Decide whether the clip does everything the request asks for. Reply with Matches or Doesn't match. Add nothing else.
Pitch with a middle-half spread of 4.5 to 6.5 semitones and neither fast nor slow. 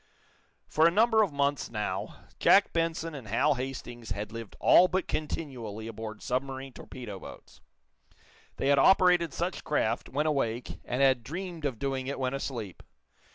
Matches